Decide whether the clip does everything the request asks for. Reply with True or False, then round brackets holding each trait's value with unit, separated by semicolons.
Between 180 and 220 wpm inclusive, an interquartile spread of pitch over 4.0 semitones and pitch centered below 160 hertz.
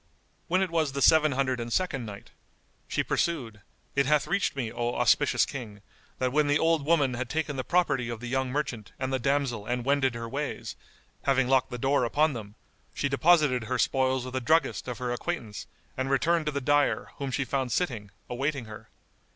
False (200 wpm; 3.2 semitones; 135 Hz)